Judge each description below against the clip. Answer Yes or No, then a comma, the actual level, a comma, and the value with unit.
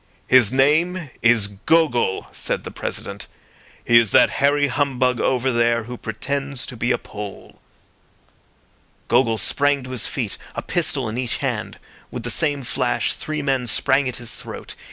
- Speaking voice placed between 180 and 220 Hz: No, low, 130 Hz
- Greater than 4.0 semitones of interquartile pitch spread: No, average, 3.3 semitones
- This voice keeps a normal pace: Yes, average, 160 wpm